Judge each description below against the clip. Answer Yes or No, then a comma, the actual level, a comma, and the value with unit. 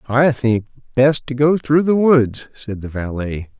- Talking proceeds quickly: No, average, 185 wpm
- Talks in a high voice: No, low, 130 Hz